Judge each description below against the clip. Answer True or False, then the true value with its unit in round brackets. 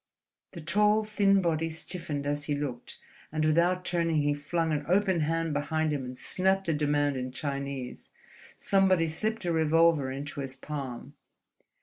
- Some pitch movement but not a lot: True (3.3 semitones)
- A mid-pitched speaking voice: True (155 Hz)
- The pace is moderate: True (155 wpm)